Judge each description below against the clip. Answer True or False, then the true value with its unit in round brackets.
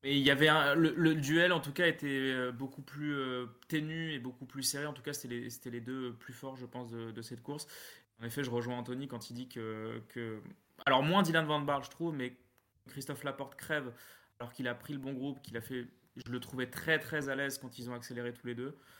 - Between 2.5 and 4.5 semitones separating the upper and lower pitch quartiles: True (3.0 semitones)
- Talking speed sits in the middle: False (255 wpm)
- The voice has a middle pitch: False (130 Hz)